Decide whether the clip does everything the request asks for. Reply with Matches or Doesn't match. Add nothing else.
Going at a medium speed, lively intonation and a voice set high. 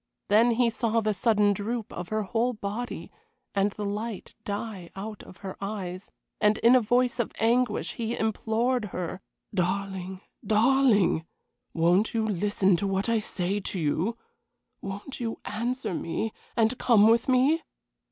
Doesn't match